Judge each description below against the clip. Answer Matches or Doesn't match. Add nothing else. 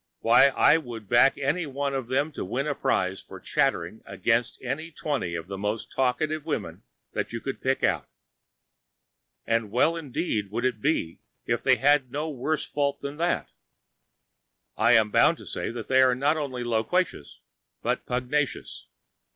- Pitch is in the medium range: Doesn't match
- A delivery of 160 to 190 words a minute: Matches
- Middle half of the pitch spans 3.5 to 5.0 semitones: Matches